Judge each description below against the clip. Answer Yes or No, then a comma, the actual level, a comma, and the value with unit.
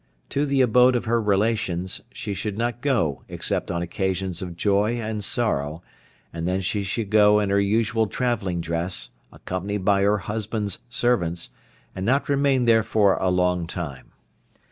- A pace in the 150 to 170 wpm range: Yes, average, 165 wpm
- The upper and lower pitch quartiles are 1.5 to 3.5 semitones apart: No, average, 4.0 semitones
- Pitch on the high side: No, low, 100 Hz